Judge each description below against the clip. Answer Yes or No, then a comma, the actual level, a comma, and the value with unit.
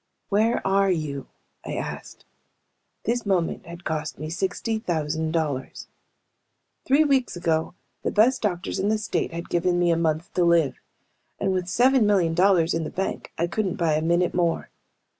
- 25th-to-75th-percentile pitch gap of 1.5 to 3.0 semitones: No, average, 3.6 semitones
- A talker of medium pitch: Yes, medium, 175 Hz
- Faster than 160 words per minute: Yes, average, 170 wpm